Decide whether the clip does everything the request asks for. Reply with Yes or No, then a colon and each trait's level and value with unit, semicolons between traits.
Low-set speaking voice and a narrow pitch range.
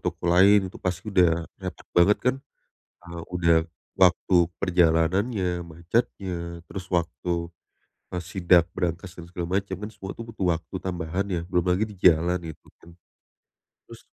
Yes: very low, 90 Hz; narrow, 2.0 semitones